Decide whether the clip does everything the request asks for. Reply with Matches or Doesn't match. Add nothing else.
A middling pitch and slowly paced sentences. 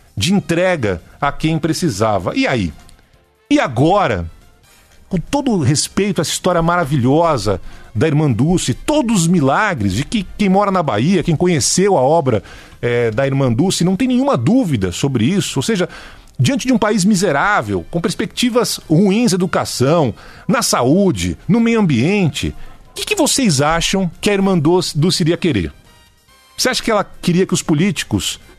Doesn't match